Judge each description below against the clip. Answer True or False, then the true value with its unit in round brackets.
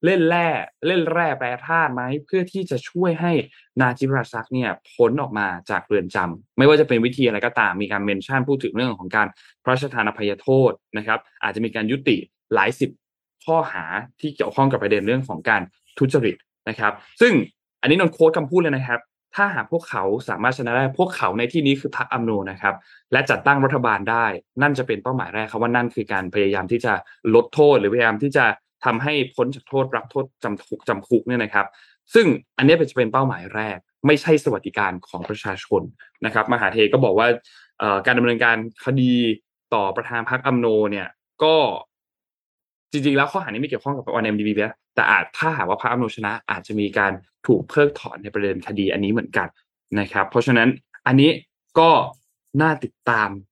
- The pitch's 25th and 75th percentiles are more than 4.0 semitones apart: True (5.0 semitones)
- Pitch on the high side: False (125 Hz)